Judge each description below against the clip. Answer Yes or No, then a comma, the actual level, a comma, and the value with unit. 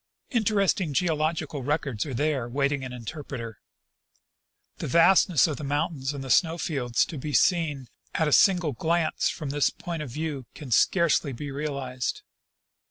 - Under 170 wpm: Yes, average, 155 wpm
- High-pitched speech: No, medium, 145 Hz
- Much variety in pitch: No, average, 3.3 semitones